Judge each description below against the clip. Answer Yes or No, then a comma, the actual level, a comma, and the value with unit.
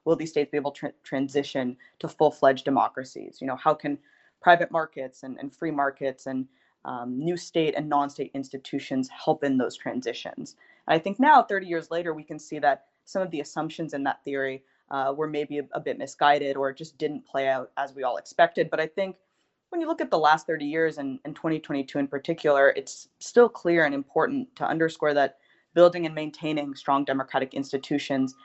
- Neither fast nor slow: No, fast, 205 wpm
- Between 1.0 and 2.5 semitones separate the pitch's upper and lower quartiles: No, average, 2.9 semitones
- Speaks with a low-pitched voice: No, medium, 145 Hz